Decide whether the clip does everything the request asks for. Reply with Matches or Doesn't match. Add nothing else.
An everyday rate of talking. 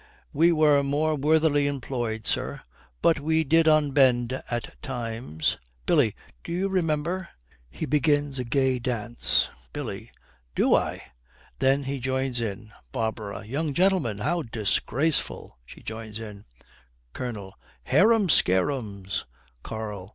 Doesn't match